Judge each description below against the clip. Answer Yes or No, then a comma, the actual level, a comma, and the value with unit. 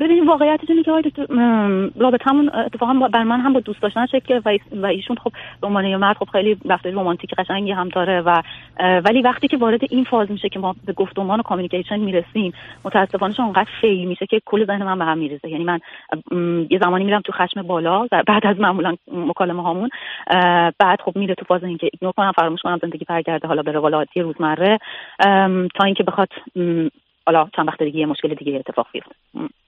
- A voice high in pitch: Yes, high, 195 Hz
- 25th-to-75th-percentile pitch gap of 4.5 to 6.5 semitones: No, average, 3.8 semitones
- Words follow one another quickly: Yes, fast, 205 wpm